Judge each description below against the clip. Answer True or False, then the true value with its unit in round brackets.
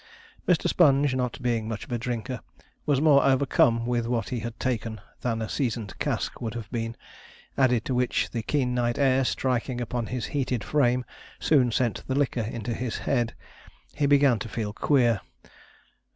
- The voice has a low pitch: True (125 Hz)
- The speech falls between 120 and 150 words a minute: False (175 wpm)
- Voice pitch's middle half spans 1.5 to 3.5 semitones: True (2.4 semitones)